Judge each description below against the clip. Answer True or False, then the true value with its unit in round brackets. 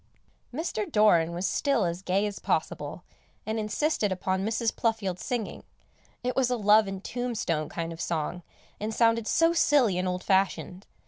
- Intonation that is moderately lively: True (4.1 semitones)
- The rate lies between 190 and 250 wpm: False (160 wpm)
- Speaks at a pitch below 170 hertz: False (210 Hz)